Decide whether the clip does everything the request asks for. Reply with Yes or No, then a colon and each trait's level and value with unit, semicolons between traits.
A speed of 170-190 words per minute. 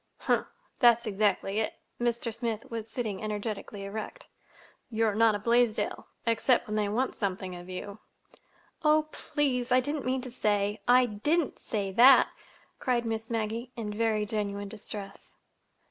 No: slow, 135 wpm